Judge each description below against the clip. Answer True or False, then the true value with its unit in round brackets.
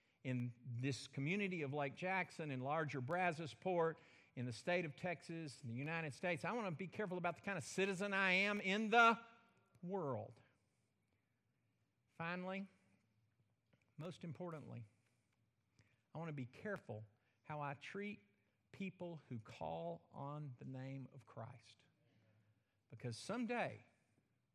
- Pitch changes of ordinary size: False (7.2 semitones)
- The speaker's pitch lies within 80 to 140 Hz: True (135 Hz)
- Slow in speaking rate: True (130 wpm)